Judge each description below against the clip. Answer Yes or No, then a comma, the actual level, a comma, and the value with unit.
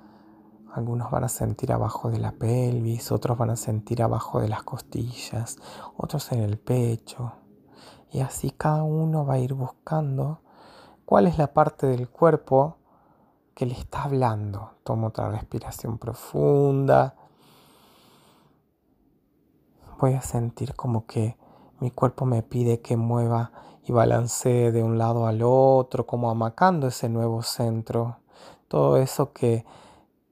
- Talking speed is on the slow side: No, average, 135 wpm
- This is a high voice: No, low, 120 Hz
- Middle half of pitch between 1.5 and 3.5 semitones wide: Yes, narrow, 2.6 semitones